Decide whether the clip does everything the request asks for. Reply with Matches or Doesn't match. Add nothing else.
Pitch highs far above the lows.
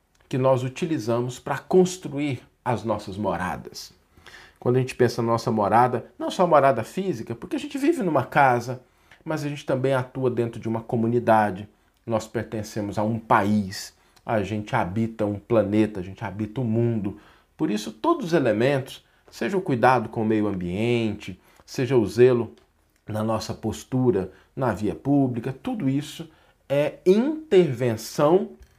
Doesn't match